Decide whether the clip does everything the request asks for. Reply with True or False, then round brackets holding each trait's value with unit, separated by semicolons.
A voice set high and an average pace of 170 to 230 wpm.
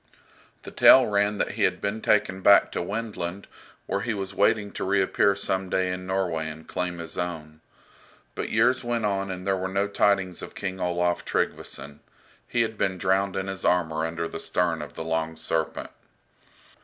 False (95 Hz; 185 wpm)